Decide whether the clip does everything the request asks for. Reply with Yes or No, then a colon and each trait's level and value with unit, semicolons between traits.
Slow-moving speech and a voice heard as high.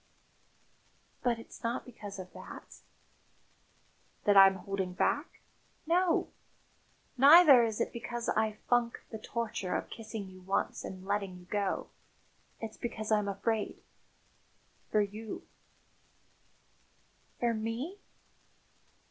Yes: slow, 115 wpm; high, 220 Hz